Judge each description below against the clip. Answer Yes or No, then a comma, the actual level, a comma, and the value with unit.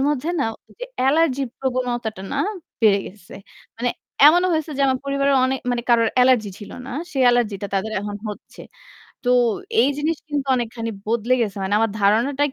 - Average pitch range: Yes, average, 4.0 semitones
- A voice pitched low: No, high, 245 Hz